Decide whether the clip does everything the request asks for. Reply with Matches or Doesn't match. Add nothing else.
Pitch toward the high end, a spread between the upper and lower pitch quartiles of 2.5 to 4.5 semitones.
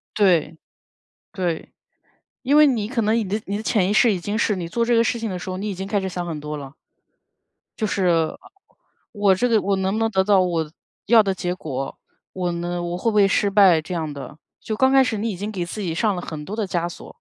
Matches